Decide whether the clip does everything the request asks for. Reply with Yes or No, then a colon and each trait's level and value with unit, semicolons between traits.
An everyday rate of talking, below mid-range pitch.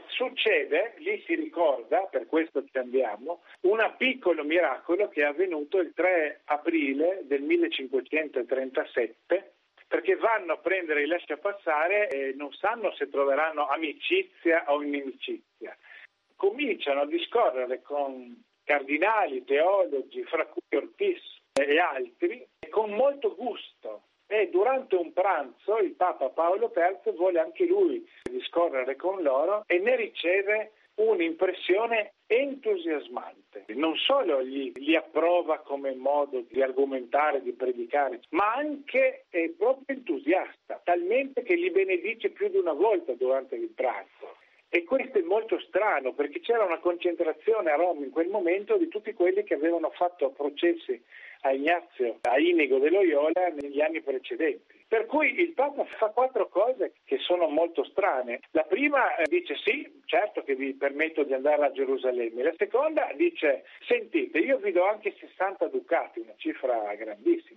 No: average, 140 wpm; high, 225 Hz